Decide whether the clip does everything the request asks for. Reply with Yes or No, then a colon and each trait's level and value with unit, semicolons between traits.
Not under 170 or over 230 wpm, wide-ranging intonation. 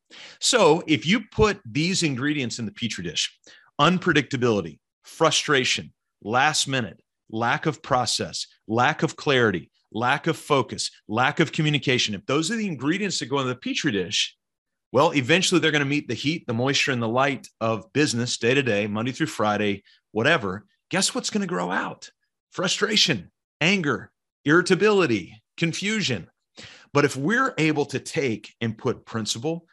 No: average, 155 wpm; wide, 5.9 semitones